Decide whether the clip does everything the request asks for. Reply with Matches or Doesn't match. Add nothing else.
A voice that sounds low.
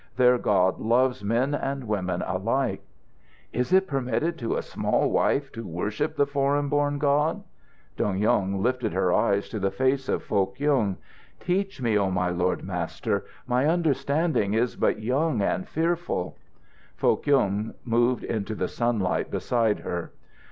Matches